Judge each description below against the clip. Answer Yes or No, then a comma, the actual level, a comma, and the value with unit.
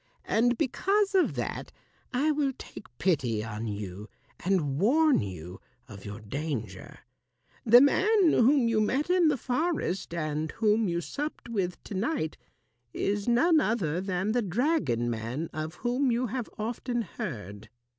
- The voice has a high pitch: Yes, high, 205 Hz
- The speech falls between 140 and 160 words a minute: Yes, average, 145 wpm